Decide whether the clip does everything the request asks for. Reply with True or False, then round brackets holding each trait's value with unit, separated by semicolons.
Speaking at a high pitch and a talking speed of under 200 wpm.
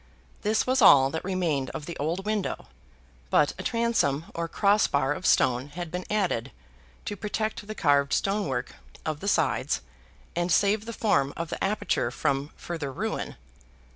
False (170 Hz; 170 wpm)